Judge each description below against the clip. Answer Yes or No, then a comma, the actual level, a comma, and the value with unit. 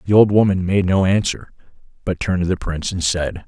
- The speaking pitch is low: Yes, very low, 90 Hz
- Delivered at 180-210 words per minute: No, fast, 225 wpm